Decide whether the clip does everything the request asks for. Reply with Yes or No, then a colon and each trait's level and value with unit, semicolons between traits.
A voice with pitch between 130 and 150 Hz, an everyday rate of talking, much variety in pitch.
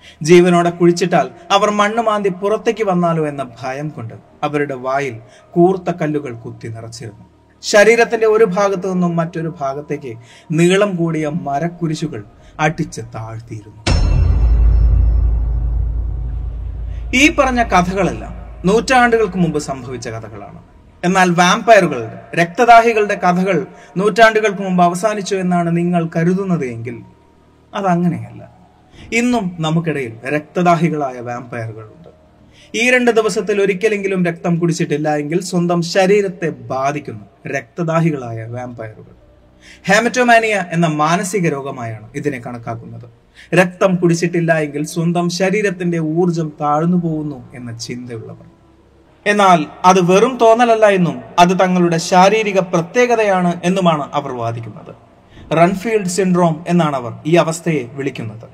No: medium, 170 Hz; average, 100 wpm; wide, 6.7 semitones